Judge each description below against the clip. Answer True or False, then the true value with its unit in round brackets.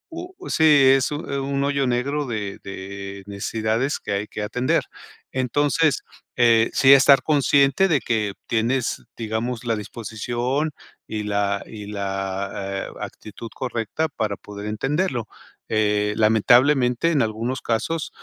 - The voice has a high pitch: False (115 Hz)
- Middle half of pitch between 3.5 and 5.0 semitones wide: True (4.7 semitones)